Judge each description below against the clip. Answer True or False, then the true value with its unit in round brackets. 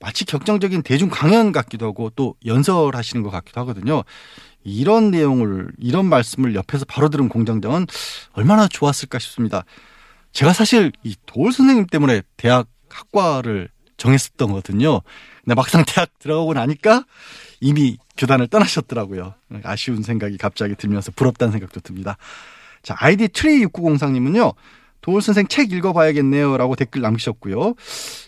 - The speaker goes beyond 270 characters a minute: True (350 characters per minute)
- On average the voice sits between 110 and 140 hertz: True (135 Hz)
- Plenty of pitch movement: True (6.8 semitones)